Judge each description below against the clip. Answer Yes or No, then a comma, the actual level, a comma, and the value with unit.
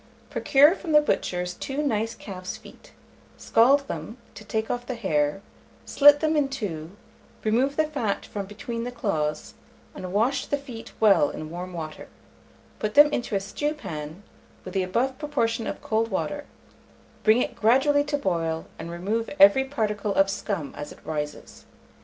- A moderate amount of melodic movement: No, wide, 6.8 semitones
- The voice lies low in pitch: No, high, 220 Hz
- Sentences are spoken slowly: No, average, 165 wpm